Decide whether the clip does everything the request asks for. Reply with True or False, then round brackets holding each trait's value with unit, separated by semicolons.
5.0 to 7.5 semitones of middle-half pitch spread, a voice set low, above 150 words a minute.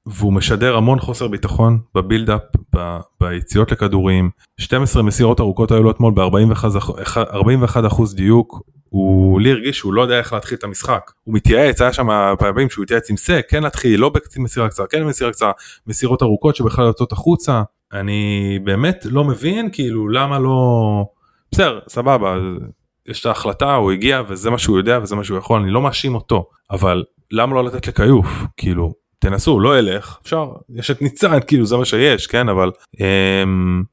False (4.3 semitones; 110 Hz; 170 wpm)